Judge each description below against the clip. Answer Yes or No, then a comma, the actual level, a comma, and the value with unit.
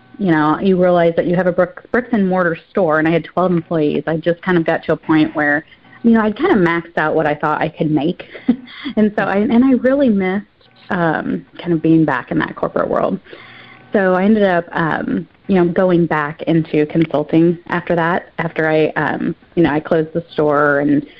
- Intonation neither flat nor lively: Yes, average, 3.2 semitones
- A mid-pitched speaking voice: Yes, medium, 170 Hz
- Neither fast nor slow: No, fast, 225 wpm